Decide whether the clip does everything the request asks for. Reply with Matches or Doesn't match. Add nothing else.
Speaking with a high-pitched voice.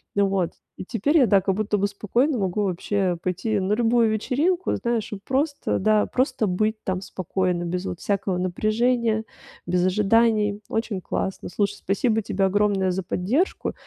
Matches